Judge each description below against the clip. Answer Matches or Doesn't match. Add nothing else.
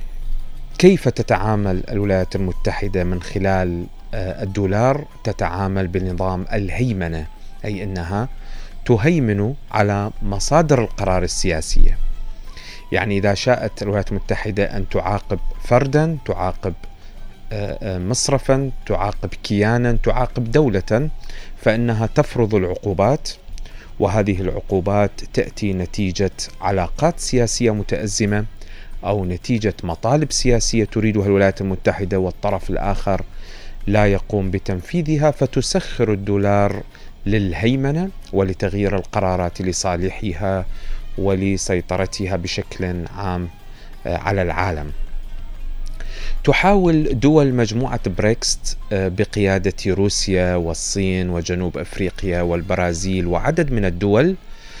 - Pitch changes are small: Doesn't match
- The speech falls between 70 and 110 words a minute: Matches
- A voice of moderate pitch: Doesn't match